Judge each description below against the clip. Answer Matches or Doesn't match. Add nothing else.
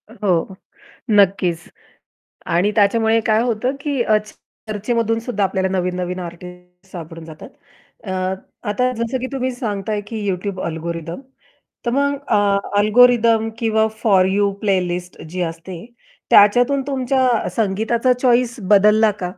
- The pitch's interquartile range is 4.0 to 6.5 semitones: Matches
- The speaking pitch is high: Matches